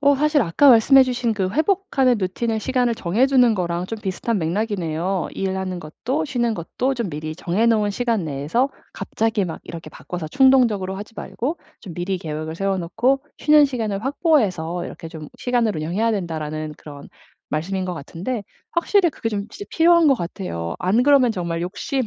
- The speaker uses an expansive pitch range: Yes, wide, 6.8 semitones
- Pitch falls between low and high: No, high, 205 Hz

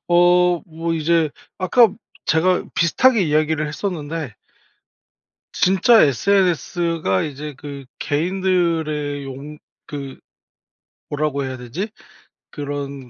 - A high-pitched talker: No, medium, 155 Hz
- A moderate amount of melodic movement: Yes, average, 3.7 semitones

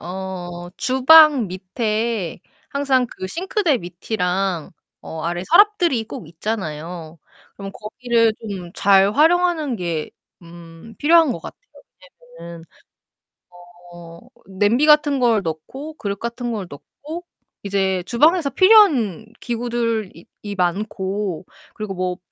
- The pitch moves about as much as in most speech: No, wide, 6.6 semitones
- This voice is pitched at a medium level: No, high, 210 Hz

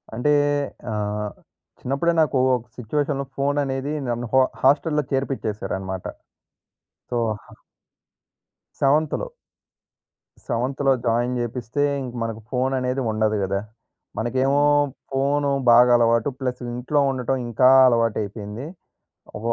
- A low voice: Yes, low, 125 Hz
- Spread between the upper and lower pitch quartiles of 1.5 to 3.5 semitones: Yes, average, 3.2 semitones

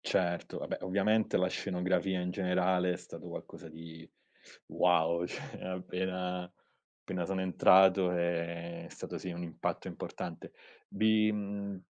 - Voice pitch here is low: Yes, very low, 90 Hz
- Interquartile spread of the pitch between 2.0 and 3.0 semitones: No, narrow, 1.6 semitones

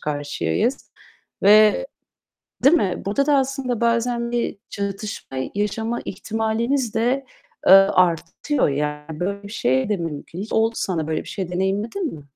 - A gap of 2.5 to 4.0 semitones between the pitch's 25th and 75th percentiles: No, average, 5.2 semitones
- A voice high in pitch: Yes, high, 210 Hz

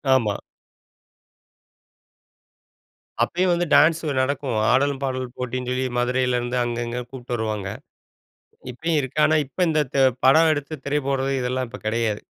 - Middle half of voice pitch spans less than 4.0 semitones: Yes, average, 2.8 semitones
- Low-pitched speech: Yes, low, 130 Hz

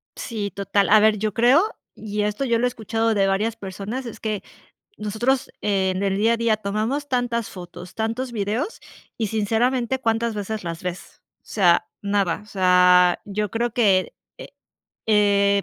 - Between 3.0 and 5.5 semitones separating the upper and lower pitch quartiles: No, narrow, 2.6 semitones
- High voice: Yes, high, 210 Hz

